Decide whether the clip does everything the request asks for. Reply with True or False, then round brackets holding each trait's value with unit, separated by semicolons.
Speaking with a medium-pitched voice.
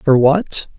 True (150 Hz)